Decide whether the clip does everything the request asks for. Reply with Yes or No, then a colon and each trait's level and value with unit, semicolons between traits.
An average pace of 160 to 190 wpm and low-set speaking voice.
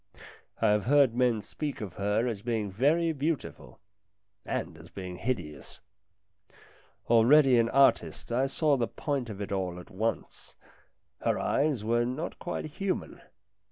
No: average, 145 wpm; low, 120 Hz